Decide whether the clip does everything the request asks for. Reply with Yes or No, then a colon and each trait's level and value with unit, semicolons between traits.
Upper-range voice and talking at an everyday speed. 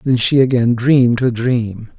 No: low, 120 Hz; average, 180 wpm